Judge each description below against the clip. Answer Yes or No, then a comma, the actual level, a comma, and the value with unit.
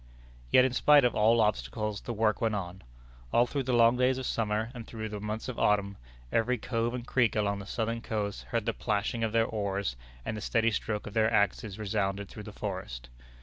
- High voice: No, low, 110 Hz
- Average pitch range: No, narrow, 2.2 semitones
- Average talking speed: No, fast, 215 wpm